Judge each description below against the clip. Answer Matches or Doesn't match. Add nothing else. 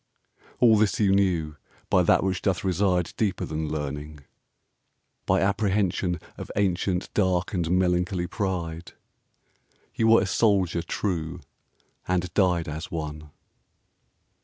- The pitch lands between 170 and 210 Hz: Doesn't match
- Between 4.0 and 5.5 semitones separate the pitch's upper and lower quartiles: Doesn't match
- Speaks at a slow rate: Matches